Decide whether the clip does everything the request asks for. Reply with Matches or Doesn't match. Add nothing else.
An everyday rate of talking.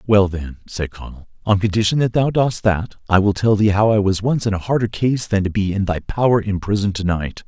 Doesn't match